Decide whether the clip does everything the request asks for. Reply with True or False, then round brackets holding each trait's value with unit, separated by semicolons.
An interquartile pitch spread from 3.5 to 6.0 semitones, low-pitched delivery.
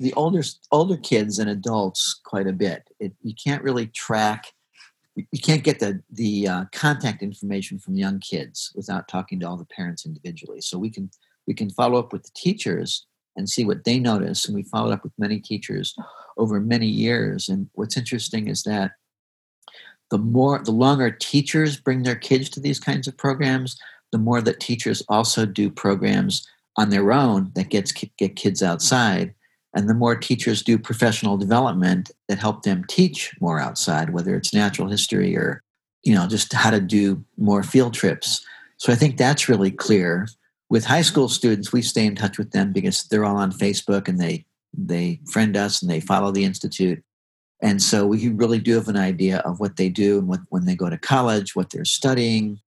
True (5.0 semitones; 110 Hz)